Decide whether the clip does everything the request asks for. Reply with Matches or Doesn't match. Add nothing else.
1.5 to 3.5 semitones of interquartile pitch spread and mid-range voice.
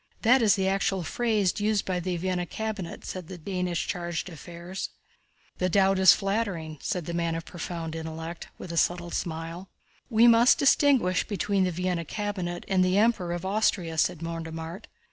Matches